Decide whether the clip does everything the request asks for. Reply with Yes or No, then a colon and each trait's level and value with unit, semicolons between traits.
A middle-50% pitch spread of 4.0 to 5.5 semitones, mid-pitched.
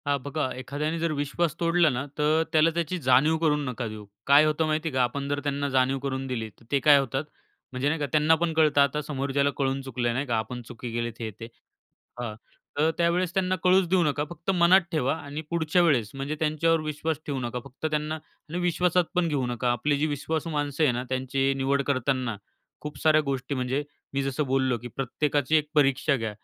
No: average, 3.2 semitones; medium, 145 Hz